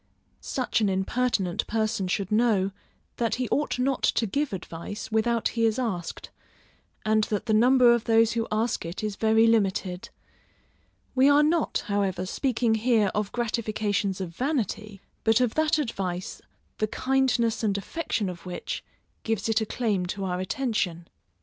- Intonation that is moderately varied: Yes, average, 3.4 semitones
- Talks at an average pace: Yes, average, 155 wpm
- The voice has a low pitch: No, high, 220 Hz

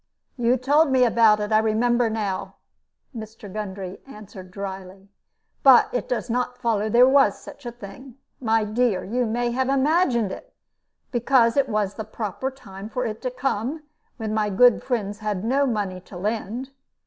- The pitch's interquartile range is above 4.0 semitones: No, average, 3.3 semitones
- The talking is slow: No, average, 170 wpm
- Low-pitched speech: No, high, 225 Hz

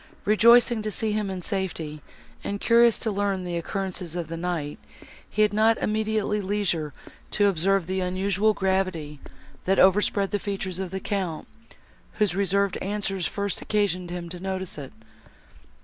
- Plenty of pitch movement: No, narrow, 2.6 semitones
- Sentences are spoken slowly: No, average, 155 wpm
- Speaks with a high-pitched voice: Yes, high, 195 Hz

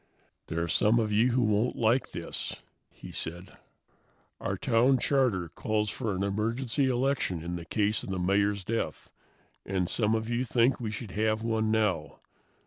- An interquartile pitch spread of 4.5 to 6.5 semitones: No, average, 3.3 semitones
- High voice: No, low, 110 Hz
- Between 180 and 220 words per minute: No, average, 165 wpm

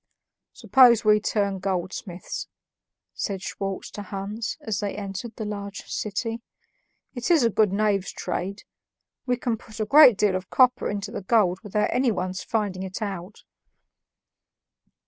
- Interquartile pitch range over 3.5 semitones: No, narrow, 2.6 semitones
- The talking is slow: No, average, 145 wpm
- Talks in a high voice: Yes, high, 205 Hz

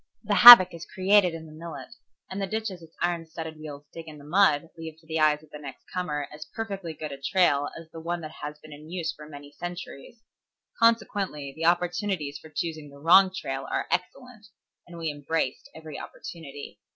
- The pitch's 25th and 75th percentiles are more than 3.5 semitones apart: No, average, 3.2 semitones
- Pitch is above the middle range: No, medium, 160 Hz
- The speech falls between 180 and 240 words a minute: Yes, average, 200 wpm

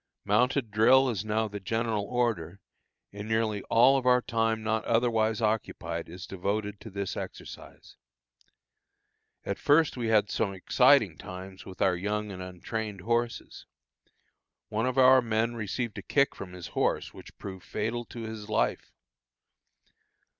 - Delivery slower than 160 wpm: Yes, average, 145 wpm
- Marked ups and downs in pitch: No, average, 2.8 semitones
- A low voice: Yes, low, 110 Hz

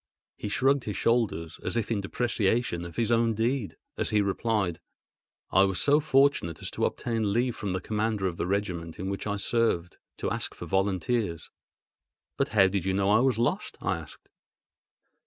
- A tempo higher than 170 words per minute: Yes, average, 185 wpm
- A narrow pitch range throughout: No, average, 3.5 semitones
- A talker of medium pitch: No, low, 105 Hz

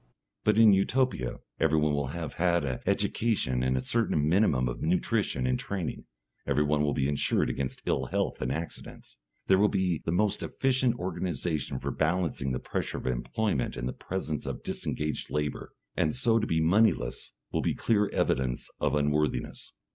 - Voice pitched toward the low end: Yes, very low, 80 Hz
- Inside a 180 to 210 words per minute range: No, average, 170 wpm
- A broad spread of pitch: Yes, wide, 6.2 semitones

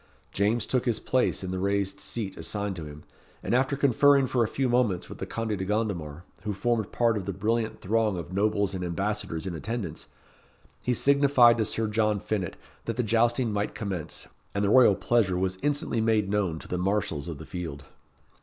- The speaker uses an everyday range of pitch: Yes, average, 4.0 semitones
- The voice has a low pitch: Yes, low, 105 Hz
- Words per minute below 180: No, average, 200 wpm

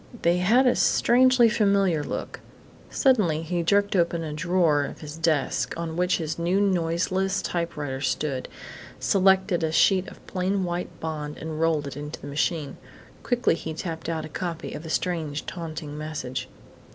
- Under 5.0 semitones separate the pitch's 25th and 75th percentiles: Yes, average, 3.3 semitones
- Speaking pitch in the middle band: Yes, medium, 165 Hz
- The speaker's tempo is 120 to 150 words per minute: No, average, 165 wpm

